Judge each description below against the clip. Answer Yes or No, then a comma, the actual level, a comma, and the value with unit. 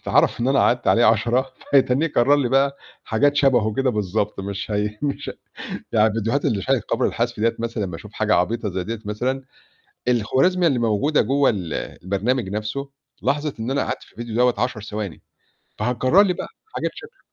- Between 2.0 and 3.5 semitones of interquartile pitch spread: No, average, 4.2 semitones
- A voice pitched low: Yes, low, 120 Hz